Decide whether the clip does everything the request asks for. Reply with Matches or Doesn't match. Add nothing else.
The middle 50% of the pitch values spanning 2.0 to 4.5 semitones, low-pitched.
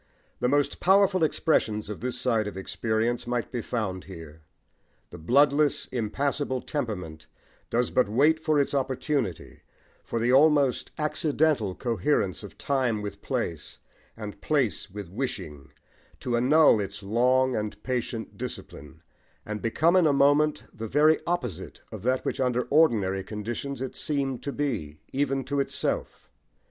Doesn't match